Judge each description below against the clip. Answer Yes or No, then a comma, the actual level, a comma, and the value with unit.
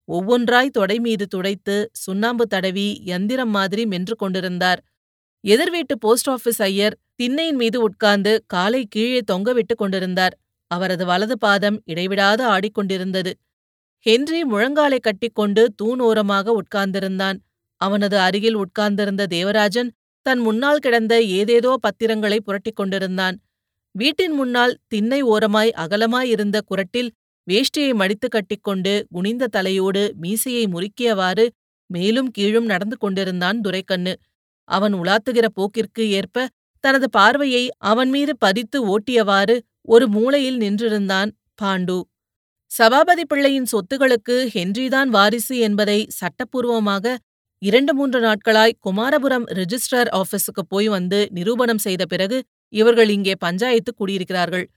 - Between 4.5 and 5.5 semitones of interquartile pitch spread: No, average, 3.7 semitones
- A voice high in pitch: Yes, high, 215 Hz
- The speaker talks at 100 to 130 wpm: Yes, average, 105 wpm